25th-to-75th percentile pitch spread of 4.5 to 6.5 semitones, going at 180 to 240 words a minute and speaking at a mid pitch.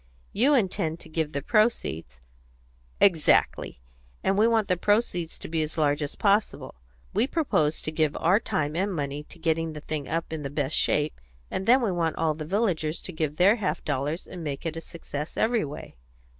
Yes: average, 4.8 semitones; average, 200 wpm; medium, 160 Hz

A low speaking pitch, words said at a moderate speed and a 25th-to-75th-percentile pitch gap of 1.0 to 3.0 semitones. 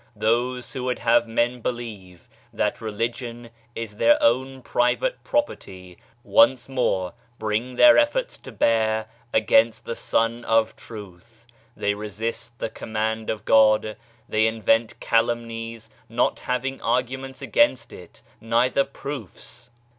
No: low, 115 Hz; slow, 125 wpm; narrow, 2.4 semitones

